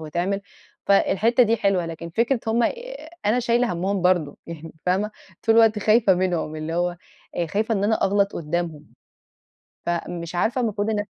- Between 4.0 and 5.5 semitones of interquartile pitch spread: Yes, average, 4.3 semitones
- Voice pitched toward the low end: No, high, 195 Hz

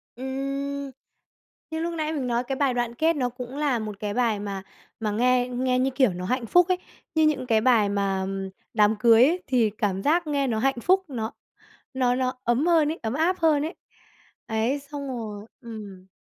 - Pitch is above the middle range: Yes, very high, 255 Hz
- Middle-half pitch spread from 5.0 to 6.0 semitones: No, average, 4.4 semitones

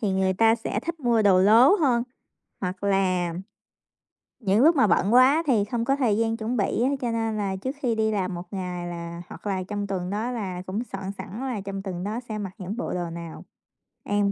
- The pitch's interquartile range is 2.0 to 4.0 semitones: Yes, average, 3.6 semitones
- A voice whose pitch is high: Yes, high, 205 Hz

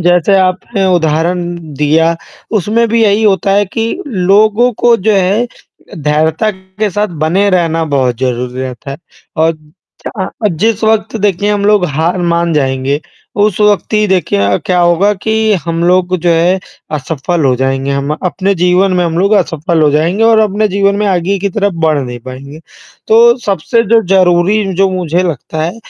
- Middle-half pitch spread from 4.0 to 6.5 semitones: Yes, average, 4.5 semitones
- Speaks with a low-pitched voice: No, medium, 180 Hz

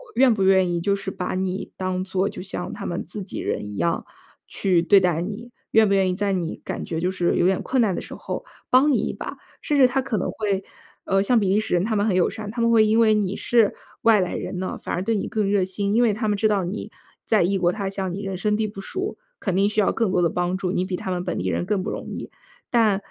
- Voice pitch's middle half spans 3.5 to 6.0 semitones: No, average, 2.8 semitones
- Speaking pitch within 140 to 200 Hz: Yes, high, 195 Hz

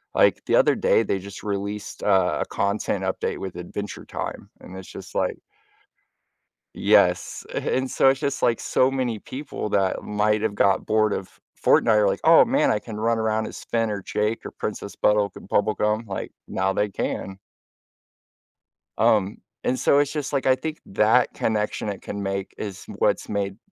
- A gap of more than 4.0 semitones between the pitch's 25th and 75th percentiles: No, average, 2.9 semitones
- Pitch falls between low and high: No, low, 105 Hz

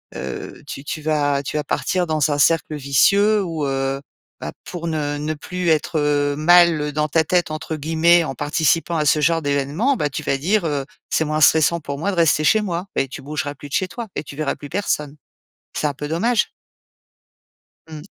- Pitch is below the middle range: No, medium, 155 Hz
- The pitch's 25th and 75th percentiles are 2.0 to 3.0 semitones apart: Yes, average, 2.7 semitones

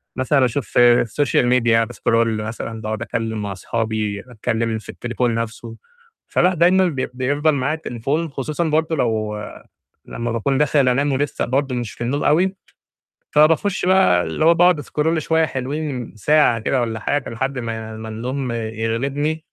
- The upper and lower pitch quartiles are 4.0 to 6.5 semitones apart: Yes, average, 4.7 semitones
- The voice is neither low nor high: No, low, 125 Hz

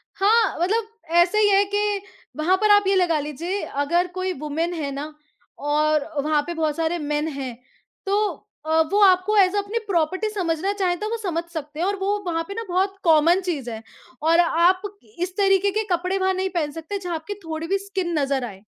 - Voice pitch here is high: Yes, very high, 350 Hz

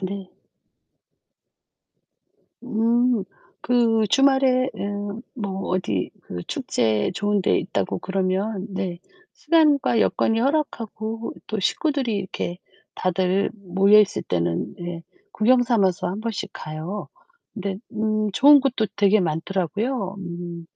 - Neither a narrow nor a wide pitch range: Yes, average, 4.1 semitones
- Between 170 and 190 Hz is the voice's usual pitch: No, high, 205 Hz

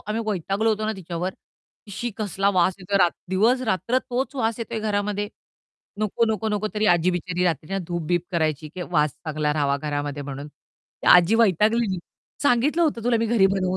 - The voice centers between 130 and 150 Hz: No, high, 195 Hz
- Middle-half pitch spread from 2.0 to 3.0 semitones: No, average, 4.6 semitones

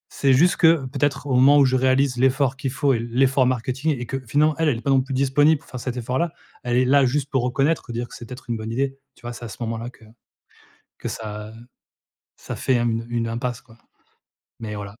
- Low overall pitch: Yes, low, 130 Hz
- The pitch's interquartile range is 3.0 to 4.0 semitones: No, narrow, 2.5 semitones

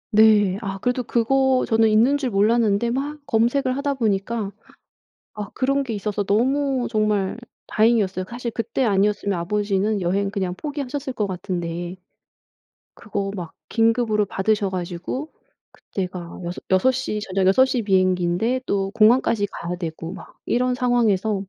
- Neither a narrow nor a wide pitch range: Yes, average, 4.1 semitones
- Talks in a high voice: Yes, high, 215 Hz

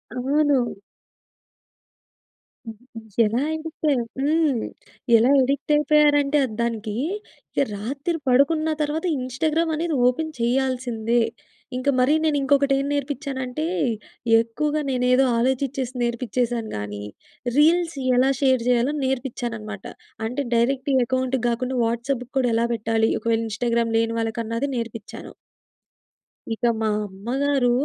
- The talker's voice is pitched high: Yes, very high, 255 Hz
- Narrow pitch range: No, average, 3.5 semitones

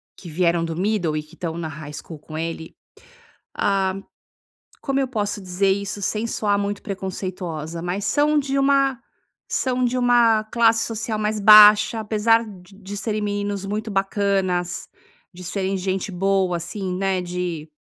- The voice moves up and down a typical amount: Yes, average, 3.3 semitones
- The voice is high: Yes, high, 195 Hz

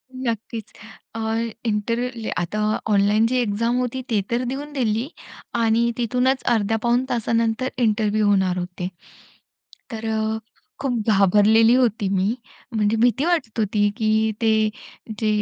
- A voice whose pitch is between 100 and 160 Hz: No, high, 225 Hz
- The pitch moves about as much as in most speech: No, narrow, 2.3 semitones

